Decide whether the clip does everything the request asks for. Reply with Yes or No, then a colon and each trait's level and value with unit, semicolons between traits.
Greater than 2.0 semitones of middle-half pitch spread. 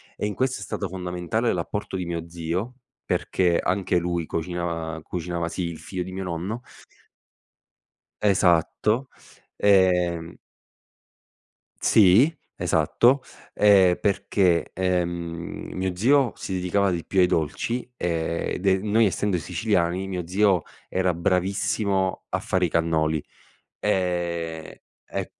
Yes: average, 2.7 semitones